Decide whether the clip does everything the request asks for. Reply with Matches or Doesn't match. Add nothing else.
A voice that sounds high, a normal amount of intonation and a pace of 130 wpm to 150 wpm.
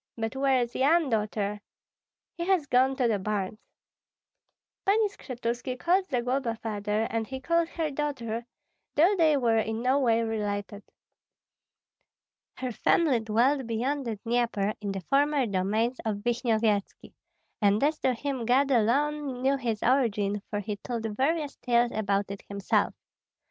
Matches